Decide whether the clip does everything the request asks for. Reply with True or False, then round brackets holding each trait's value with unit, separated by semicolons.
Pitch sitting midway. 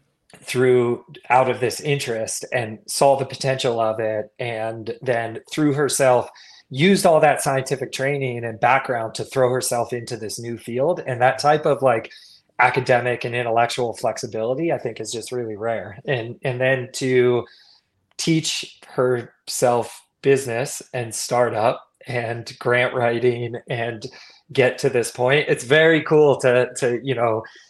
False (125 Hz)